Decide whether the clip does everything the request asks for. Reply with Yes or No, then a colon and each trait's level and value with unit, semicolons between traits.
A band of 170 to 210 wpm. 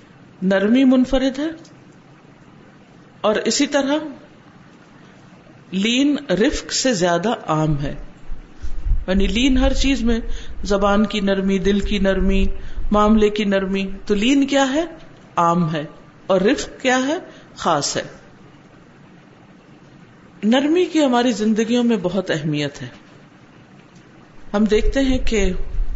No: average, 115 wpm